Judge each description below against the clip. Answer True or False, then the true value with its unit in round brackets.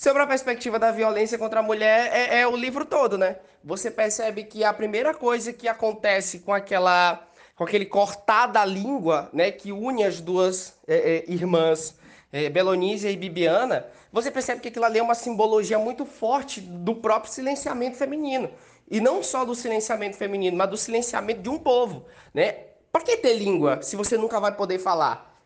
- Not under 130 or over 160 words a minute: False (185 wpm)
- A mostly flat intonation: False (3.9 semitones)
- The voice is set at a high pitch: True (220 Hz)